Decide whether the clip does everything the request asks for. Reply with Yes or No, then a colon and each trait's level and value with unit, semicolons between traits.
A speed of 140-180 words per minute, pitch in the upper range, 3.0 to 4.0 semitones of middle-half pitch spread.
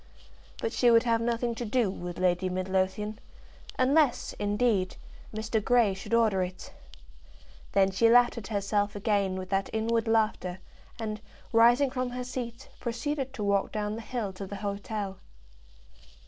Yes: average, 150 wpm; high, 215 Hz; average, 3.3 semitones